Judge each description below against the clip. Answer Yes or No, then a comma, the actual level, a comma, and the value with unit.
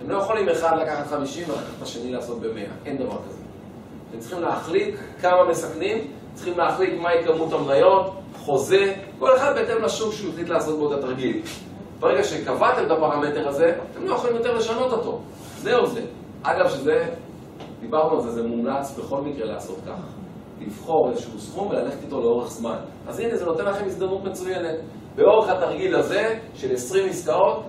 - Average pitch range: No, wide, 6.6 semitones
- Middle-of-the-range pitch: Yes, medium, 170 Hz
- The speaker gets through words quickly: Yes, fast, 170 wpm